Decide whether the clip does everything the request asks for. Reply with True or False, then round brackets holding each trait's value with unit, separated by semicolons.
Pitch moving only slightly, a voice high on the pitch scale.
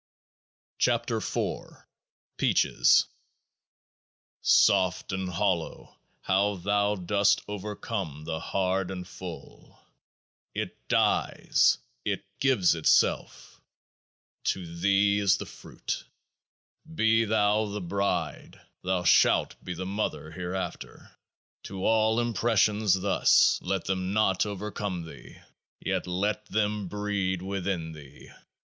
False (2.3 semitones; 95 Hz)